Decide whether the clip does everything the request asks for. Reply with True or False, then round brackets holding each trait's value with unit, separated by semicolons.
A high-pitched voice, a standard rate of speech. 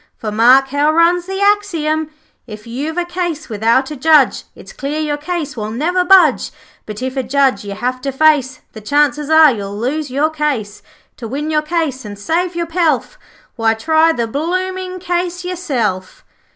True (295 Hz; 180 wpm)